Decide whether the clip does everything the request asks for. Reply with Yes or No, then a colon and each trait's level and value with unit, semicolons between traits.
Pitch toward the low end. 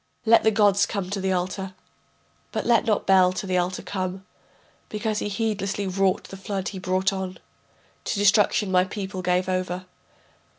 No: high, 190 Hz